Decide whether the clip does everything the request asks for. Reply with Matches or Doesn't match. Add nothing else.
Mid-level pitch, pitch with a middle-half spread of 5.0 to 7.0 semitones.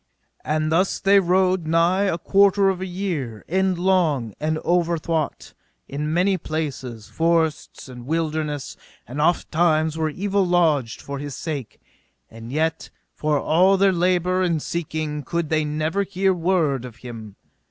Doesn't match